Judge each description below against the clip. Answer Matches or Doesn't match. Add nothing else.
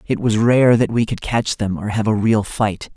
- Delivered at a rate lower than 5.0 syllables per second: Matches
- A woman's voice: Doesn't match